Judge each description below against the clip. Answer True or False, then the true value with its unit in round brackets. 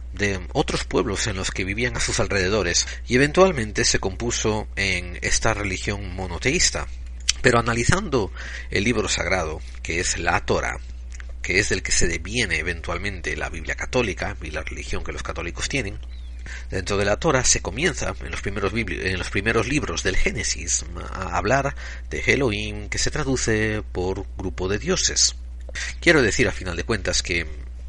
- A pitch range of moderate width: False (8.1 semitones)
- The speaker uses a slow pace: False (170 wpm)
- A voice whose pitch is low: True (90 Hz)